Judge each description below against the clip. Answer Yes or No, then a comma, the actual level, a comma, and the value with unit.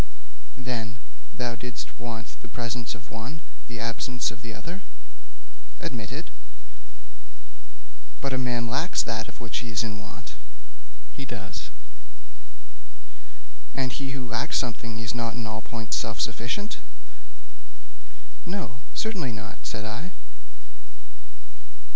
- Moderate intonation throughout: No, narrow, 2.3 semitones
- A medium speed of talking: No, slow, 125 wpm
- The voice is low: Yes, low, 120 Hz